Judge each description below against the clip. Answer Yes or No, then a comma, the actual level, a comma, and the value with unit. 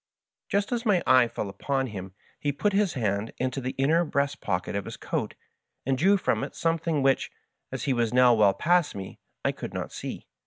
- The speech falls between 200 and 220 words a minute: Yes, fast, 205 wpm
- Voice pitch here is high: No, low, 135 Hz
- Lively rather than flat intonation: Yes, wide, 6.9 semitones